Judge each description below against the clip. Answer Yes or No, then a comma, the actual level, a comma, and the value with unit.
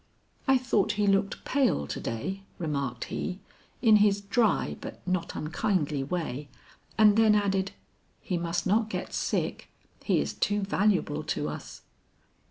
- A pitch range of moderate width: Yes, average, 4.3 semitones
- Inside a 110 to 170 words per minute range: Yes, average, 145 wpm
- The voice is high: Yes, high, 195 Hz